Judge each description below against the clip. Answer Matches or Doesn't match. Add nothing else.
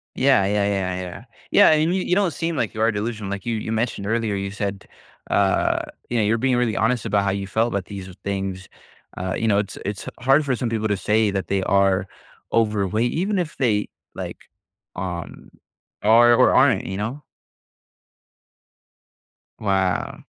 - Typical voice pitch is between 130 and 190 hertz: Doesn't match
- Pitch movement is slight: Doesn't match